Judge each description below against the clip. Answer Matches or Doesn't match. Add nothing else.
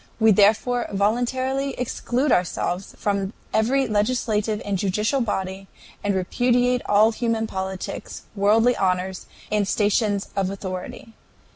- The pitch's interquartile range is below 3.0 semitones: Doesn't match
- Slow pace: Matches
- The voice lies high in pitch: Matches